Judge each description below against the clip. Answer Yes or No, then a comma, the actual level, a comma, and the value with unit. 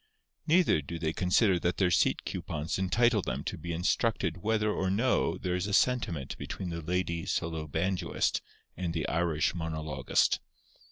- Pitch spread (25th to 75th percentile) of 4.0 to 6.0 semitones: No, average, 3.6 semitones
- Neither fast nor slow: Yes, average, 160 wpm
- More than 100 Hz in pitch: No, very low, 90 Hz